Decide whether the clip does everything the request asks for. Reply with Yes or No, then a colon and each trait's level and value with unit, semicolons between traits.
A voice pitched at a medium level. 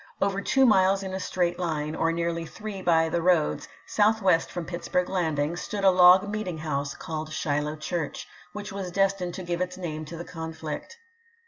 Yes: medium, 175 Hz